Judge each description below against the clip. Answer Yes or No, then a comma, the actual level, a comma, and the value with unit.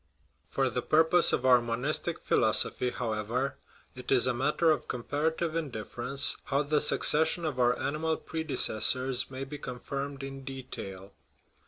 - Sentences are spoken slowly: No, average, 145 wpm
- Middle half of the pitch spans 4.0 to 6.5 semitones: No, average, 3.4 semitones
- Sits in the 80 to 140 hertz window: Yes, low, 135 Hz